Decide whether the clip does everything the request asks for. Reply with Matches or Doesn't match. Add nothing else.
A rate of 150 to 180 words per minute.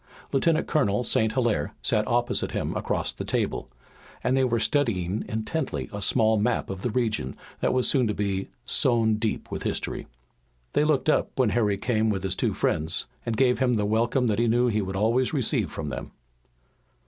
Doesn't match